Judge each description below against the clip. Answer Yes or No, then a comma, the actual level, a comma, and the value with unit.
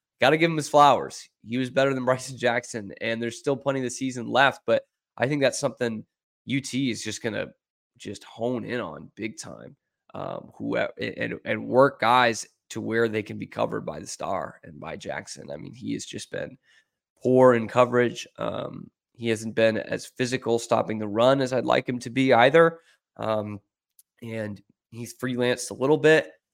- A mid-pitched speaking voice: No, low, 120 Hz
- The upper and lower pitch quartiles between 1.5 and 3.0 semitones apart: Yes, average, 2.7 semitones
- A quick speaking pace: No, average, 190 wpm